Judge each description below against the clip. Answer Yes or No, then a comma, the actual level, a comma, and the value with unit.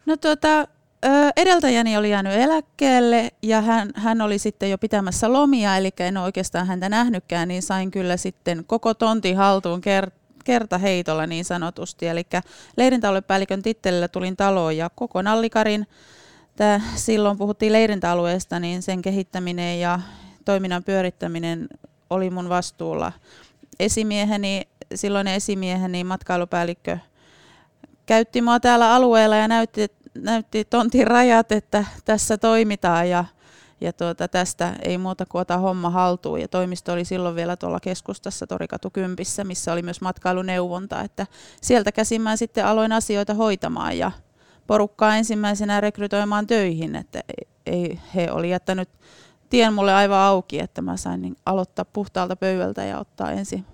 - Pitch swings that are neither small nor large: Yes, average, 3.5 semitones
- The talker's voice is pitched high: Yes, high, 195 Hz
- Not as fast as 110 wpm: No, average, 135 wpm